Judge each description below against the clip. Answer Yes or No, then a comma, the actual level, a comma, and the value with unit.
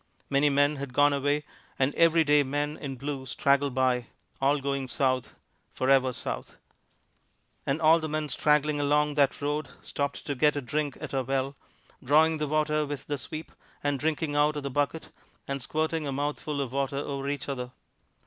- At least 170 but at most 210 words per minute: Yes, average, 180 wpm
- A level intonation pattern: Yes, narrow, 1.6 semitones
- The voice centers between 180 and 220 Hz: No, medium, 145 Hz